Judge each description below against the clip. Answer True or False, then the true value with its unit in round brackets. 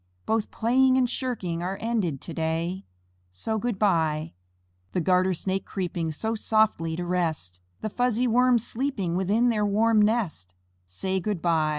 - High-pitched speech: True (195 Hz)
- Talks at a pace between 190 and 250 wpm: False (155 wpm)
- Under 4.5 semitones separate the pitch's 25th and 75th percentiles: False (5.1 semitones)